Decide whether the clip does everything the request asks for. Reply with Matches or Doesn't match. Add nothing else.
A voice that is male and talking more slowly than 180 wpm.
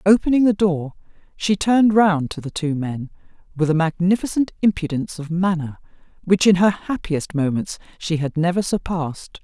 Doesn't match